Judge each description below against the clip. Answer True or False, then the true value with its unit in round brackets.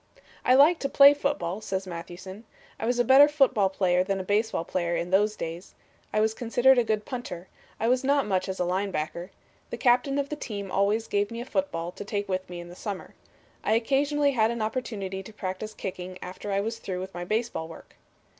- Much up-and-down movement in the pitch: False (4.7 semitones)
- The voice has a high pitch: True (210 Hz)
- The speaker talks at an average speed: False (220 wpm)